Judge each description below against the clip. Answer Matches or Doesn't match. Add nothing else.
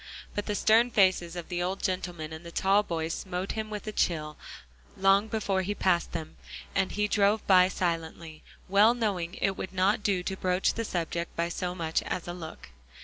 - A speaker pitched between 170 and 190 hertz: Matches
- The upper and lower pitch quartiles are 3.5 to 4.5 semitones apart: Doesn't match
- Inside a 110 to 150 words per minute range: Doesn't match